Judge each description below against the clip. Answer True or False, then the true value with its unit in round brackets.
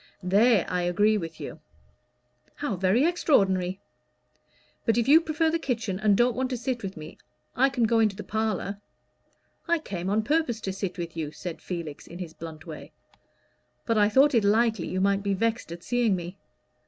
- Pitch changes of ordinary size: True (4.8 semitones)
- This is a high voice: True (205 Hz)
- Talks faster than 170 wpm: True (190 wpm)